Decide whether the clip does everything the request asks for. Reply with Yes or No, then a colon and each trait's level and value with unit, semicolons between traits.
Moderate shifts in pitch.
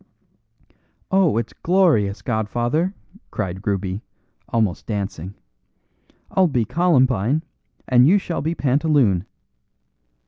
No: wide, 8.0 semitones